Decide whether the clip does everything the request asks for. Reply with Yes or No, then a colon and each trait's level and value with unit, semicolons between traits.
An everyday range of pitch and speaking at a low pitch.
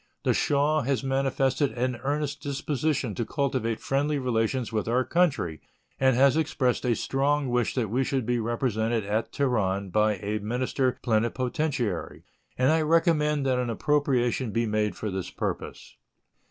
Yes: average, 3.7 semitones; low, 130 Hz